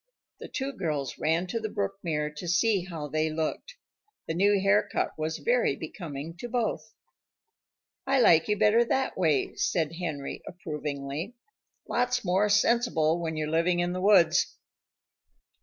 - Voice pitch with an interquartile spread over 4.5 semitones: Yes, average, 5.1 semitones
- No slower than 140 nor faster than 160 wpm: Yes, average, 150 wpm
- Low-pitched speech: No, medium, 175 Hz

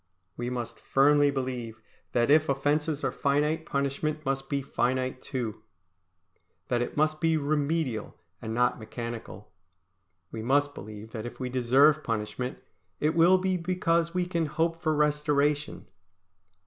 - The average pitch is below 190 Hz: Yes, medium, 140 Hz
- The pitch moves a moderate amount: Yes, average, 3.8 semitones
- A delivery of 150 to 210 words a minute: No, average, 140 wpm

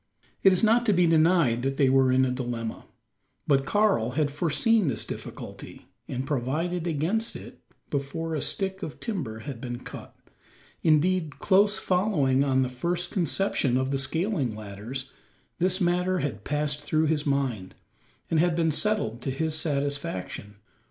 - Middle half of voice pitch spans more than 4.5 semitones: Yes, average, 5.2 semitones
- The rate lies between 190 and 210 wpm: No, average, 160 wpm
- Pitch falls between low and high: Yes, medium, 150 Hz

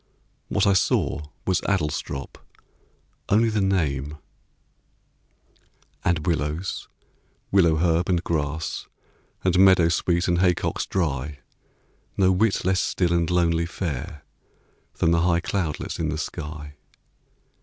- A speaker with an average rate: No, slow, 110 wpm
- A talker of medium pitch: No, very low, 85 Hz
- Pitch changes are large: No, average, 3.3 semitones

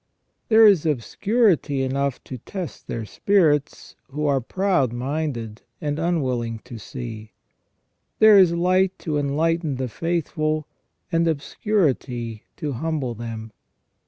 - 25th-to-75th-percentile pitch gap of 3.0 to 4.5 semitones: No, average, 5.3 semitones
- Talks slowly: Yes, slow, 120 wpm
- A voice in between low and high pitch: Yes, medium, 145 Hz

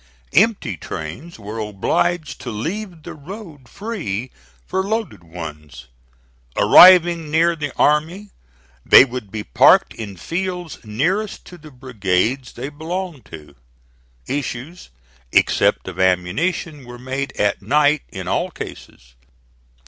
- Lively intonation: Yes, wide, 8.6 semitones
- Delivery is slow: Yes, slow, 120 wpm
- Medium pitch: Yes, medium, 145 Hz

